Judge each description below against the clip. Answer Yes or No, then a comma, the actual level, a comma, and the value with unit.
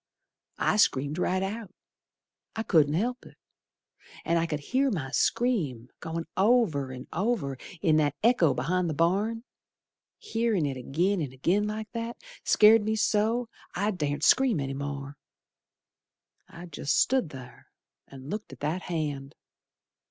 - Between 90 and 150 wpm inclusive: Yes, average, 145 wpm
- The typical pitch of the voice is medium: Yes, medium, 175 Hz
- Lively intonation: Yes, wide, 7.3 semitones